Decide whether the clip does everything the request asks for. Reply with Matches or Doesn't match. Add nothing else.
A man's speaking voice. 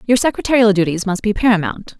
Doesn't match